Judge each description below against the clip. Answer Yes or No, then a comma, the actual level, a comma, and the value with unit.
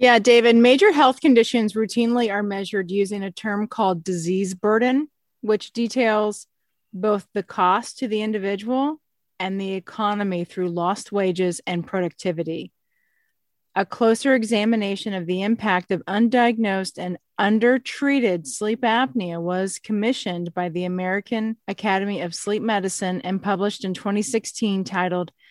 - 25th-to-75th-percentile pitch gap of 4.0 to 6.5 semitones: No, average, 3.5 semitones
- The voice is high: Yes, high, 205 Hz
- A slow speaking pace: Yes, slow, 130 wpm